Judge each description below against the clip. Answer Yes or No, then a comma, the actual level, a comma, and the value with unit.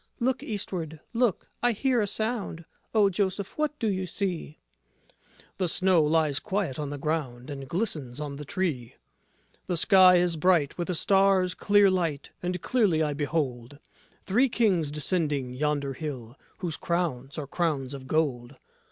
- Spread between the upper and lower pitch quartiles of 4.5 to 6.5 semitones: Yes, average, 5.0 semitones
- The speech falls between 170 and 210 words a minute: No, average, 160 wpm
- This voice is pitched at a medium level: Yes, medium, 165 Hz